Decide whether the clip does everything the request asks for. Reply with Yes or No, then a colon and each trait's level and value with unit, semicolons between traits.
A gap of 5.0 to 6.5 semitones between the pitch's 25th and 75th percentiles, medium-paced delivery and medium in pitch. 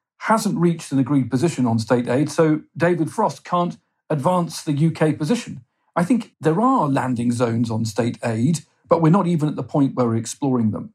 Yes: wide, 5.5 semitones; average, 195 wpm; medium, 150 Hz